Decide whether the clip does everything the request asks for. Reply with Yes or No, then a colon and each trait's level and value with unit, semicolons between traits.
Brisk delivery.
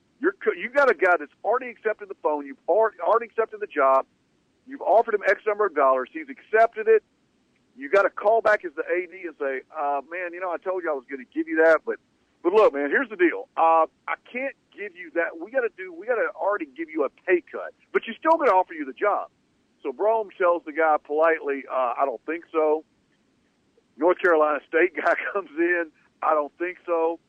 Yes: fast, 235 wpm